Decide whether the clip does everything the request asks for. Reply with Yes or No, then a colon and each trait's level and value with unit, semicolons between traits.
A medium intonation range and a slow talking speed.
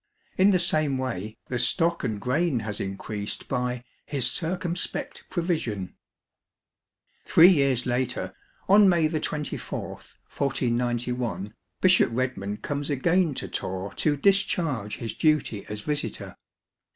No: wide, 6.3 semitones; slow, 125 wpm